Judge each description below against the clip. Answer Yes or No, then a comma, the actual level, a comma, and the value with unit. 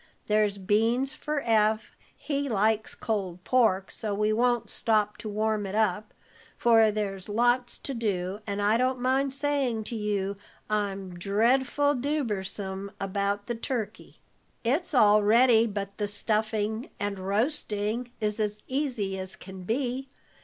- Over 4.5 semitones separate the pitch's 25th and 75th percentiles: No, average, 3.2 semitones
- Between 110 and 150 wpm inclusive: Yes, average, 140 wpm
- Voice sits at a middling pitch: No, high, 215 Hz